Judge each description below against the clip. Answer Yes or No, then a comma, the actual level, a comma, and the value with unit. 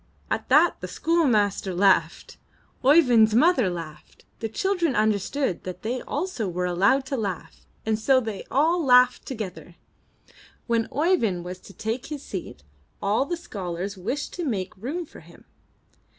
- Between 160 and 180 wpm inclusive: No, average, 150 wpm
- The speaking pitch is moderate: No, high, 225 Hz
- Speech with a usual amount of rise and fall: No, wide, 6.8 semitones